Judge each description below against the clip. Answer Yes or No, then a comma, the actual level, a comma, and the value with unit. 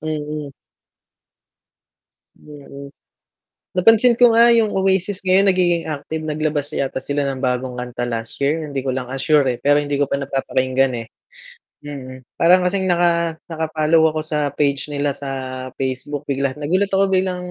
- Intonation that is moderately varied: Yes, average, 4.3 semitones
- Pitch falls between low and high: Yes, medium, 150 Hz